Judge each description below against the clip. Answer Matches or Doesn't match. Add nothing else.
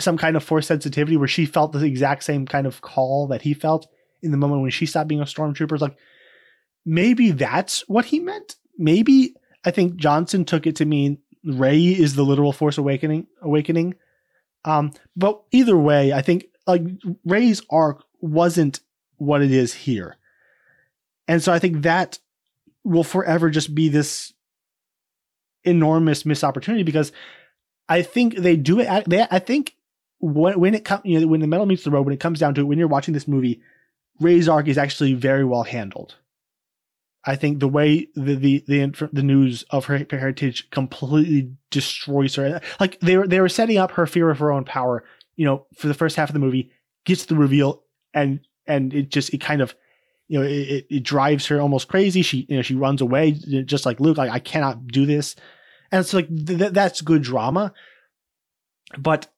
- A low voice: Doesn't match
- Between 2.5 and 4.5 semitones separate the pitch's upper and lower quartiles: Matches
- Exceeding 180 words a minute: Matches